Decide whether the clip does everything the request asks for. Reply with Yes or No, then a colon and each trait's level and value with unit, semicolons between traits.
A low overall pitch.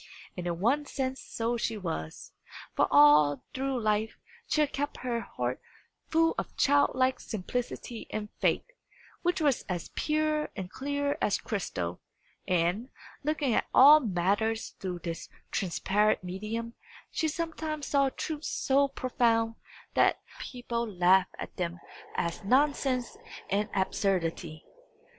No: high, 230 Hz